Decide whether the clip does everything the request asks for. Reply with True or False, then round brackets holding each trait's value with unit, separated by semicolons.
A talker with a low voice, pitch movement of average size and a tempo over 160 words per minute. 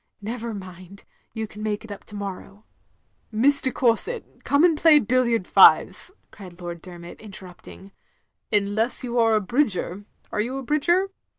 False (215 Hz; 4.5 semitones; 170 wpm)